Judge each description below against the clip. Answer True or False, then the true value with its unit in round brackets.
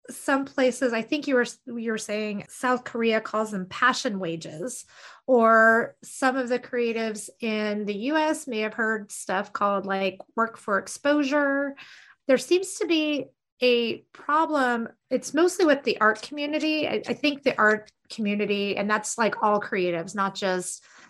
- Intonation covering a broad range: False (4.6 semitones)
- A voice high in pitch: True (230 Hz)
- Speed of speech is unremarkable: True (160 wpm)